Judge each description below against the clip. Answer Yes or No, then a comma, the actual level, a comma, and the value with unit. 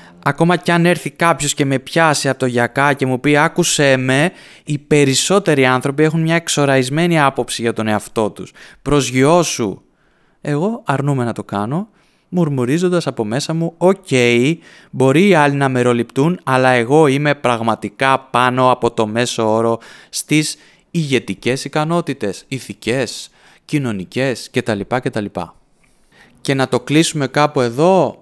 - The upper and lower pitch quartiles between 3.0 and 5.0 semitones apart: Yes, average, 4.3 semitones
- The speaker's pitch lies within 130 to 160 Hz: Yes, low, 135 Hz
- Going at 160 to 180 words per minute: No, average, 140 wpm